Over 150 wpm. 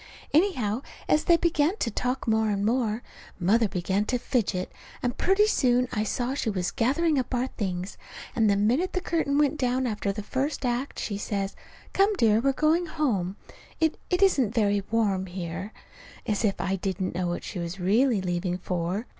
Yes: average, 185 wpm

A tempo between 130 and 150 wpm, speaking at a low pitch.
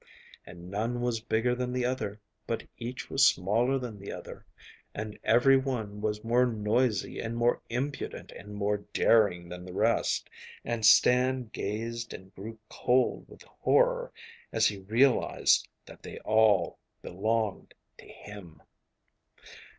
Yes: average, 140 wpm; low, 115 Hz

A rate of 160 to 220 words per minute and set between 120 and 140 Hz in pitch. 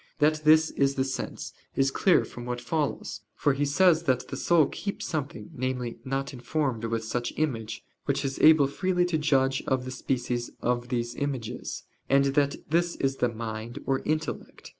Yes: average, 180 wpm; low, 135 Hz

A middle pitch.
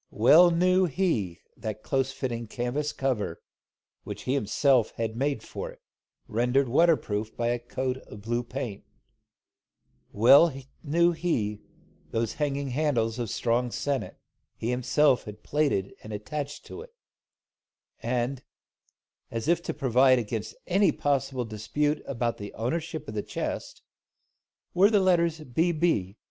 No: low, 130 Hz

